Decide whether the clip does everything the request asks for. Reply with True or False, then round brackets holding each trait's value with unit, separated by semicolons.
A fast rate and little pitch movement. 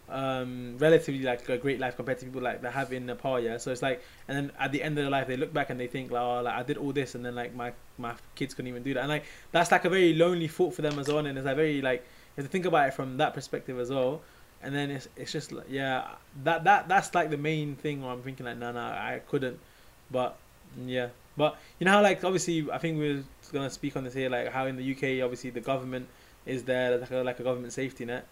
False (280 wpm; 3.0 semitones)